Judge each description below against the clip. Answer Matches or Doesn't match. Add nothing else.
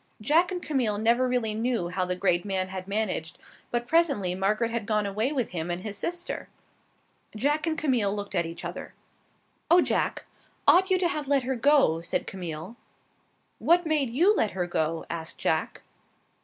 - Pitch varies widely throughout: Matches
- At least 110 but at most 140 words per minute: Doesn't match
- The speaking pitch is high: Matches